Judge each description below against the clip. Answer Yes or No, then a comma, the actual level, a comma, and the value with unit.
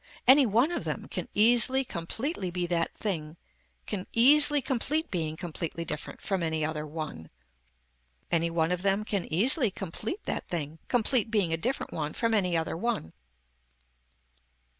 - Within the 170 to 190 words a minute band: No, average, 155 wpm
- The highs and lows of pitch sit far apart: Yes, wide, 6.6 semitones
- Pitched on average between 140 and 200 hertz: Yes, high, 190 Hz